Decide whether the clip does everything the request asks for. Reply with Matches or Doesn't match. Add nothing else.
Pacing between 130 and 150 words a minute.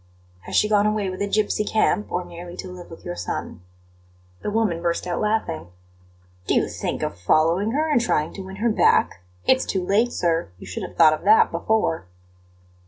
Doesn't match